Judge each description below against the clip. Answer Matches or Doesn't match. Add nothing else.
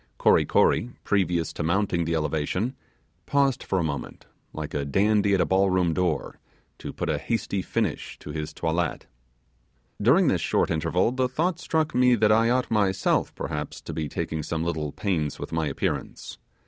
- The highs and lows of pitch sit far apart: Matches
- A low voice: Matches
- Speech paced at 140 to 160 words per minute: Doesn't match